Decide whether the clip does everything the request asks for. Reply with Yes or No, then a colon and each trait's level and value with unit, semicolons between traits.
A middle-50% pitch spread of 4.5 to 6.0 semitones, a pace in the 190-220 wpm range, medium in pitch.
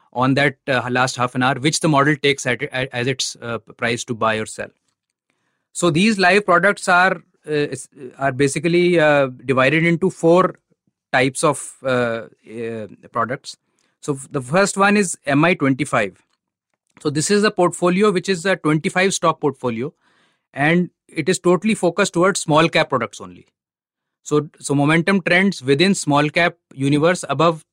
No: average, 4.9 semitones; average, 170 wpm; medium, 155 Hz